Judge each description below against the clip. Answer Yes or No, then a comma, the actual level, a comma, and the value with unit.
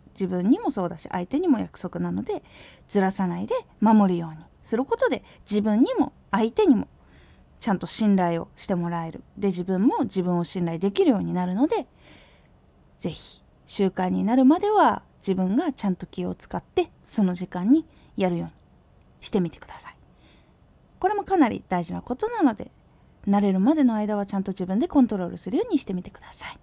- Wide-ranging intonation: Yes, wide, 7.5 semitones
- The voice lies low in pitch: No, high, 205 Hz